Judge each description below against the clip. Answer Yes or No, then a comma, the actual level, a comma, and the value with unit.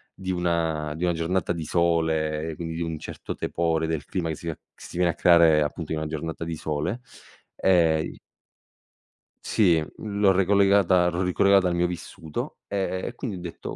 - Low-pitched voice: Yes, very low, 85 Hz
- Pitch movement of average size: No, narrow, 2.2 semitones